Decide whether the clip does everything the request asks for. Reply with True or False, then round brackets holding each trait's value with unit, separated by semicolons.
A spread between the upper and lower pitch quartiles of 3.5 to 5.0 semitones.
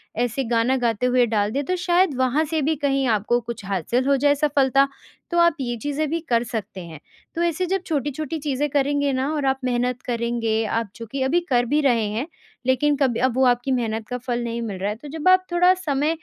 True (3.9 semitones)